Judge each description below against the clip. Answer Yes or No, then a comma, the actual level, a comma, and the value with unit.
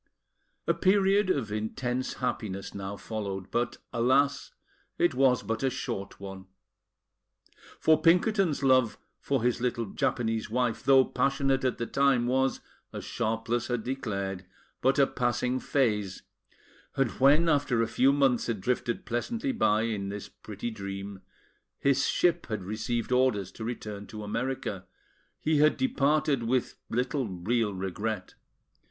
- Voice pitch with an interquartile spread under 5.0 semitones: Yes, average, 4.3 semitones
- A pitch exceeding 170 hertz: No, low, 120 Hz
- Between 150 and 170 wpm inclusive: No, average, 140 wpm